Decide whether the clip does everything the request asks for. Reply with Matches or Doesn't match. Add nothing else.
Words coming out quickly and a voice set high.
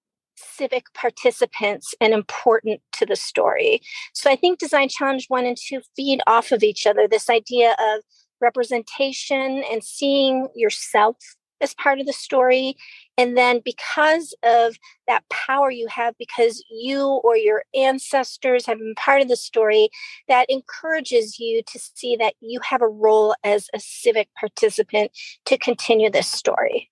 Doesn't match